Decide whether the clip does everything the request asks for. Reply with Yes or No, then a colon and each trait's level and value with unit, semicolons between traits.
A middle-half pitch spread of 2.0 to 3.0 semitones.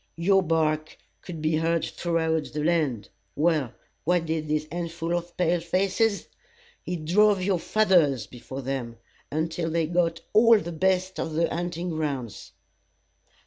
Yes: narrow, 2.4 semitones